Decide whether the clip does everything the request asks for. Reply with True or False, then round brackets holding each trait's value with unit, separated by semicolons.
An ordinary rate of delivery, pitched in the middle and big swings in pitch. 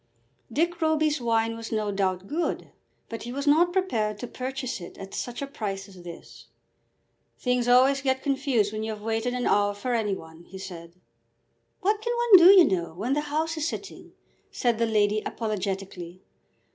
False (185 wpm; 230 Hz; 6.0 semitones)